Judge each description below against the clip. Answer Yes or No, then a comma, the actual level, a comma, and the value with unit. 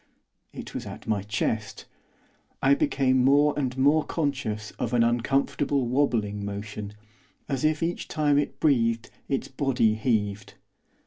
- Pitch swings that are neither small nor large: Yes, average, 4.7 semitones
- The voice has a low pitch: Yes, low, 125 Hz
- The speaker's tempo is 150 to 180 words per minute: No, slow, 135 wpm